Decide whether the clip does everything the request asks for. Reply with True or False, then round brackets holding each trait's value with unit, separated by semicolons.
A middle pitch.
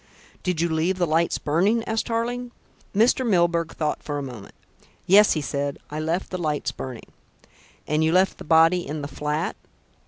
True (165 Hz)